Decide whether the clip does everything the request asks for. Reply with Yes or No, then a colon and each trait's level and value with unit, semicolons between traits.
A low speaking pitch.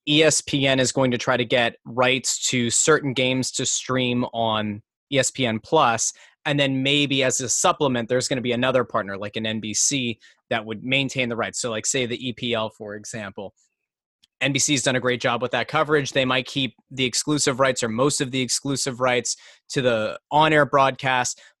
Yes: low, 130 Hz